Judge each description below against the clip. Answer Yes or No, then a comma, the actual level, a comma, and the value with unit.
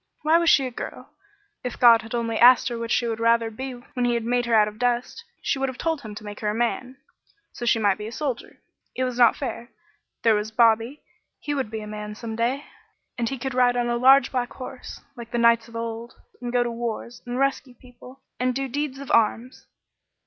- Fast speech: Yes, fast, 235 wpm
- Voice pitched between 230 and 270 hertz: Yes, high, 240 Hz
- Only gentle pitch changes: Yes, narrow, 2.0 semitones